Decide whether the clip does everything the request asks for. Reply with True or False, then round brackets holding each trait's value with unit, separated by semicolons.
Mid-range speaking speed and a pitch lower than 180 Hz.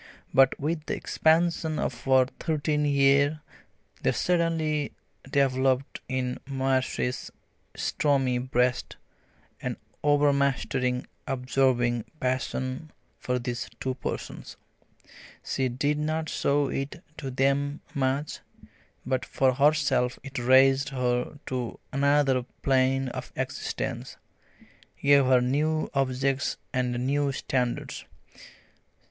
False (100 wpm; 135 Hz)